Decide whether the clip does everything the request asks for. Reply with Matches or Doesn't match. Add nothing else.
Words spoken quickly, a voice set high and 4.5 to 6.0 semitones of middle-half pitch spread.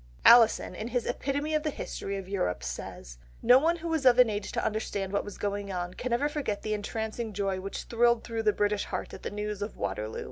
Doesn't match